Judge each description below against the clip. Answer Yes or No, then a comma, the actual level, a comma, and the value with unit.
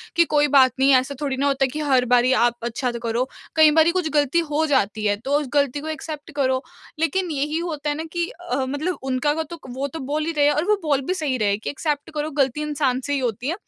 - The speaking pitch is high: Yes, very high, 285 Hz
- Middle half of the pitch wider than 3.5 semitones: No, average, 2.9 semitones